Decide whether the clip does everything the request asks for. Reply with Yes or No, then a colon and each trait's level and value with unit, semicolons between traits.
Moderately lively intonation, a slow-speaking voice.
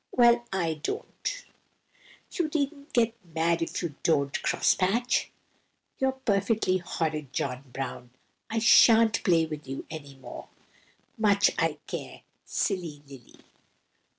No: wide, 7.1 semitones; slow, 125 wpm